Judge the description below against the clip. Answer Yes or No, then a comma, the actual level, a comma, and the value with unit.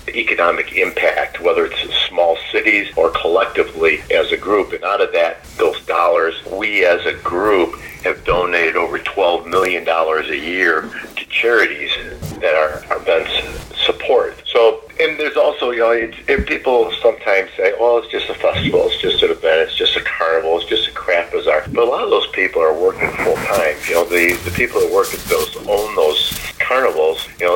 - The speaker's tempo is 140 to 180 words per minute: No, average, 190 wpm